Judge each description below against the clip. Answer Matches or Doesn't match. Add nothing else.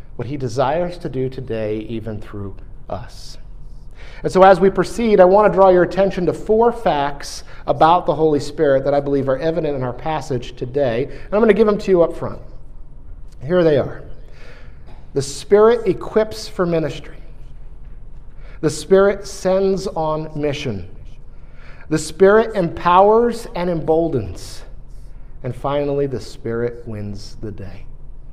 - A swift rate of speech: Doesn't match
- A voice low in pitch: Doesn't match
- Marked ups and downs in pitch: Matches